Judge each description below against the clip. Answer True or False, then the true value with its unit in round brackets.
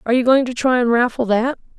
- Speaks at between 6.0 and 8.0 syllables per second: True (6.7 syllables/s)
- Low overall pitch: False (245 Hz)